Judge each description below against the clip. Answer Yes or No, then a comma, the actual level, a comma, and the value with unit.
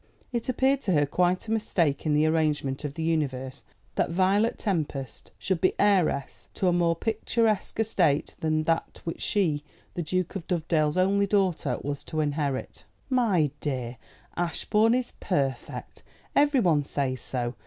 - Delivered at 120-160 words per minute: Yes, average, 155 wpm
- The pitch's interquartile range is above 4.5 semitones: Yes, wide, 5.4 semitones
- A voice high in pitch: No, medium, 165 Hz